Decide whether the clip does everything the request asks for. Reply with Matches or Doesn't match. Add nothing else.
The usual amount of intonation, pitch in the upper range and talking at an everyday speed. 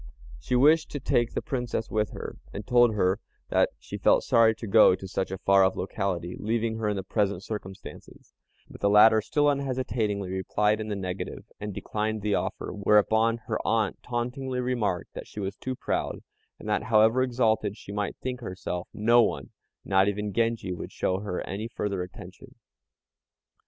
Doesn't match